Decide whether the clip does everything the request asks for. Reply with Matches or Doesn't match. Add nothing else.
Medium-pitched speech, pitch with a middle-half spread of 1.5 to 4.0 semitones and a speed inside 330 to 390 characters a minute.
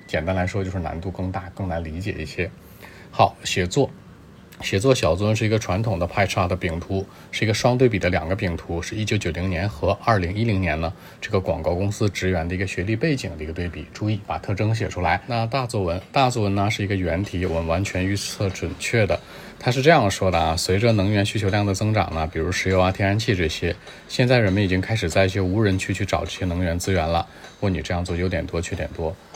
Doesn't match